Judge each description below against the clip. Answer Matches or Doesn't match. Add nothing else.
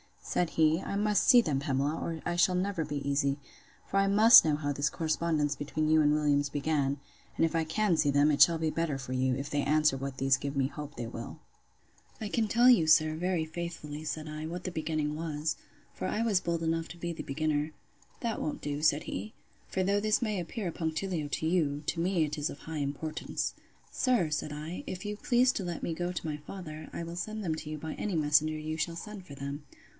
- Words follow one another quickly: Matches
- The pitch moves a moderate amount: Matches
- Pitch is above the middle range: Doesn't match